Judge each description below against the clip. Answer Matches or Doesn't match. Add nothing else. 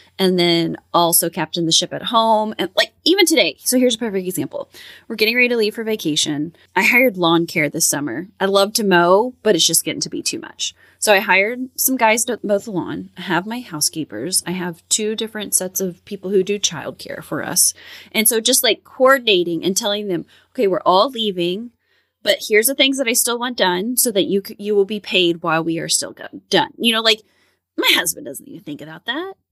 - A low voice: Doesn't match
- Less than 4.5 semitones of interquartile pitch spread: Doesn't match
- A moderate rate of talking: Doesn't match